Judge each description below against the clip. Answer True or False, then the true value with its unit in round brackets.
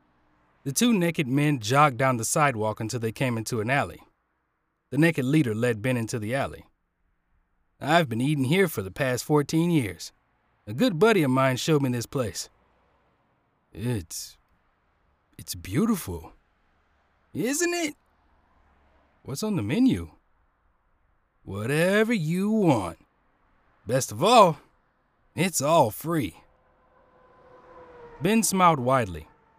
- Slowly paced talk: True (125 wpm)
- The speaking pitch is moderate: False (125 Hz)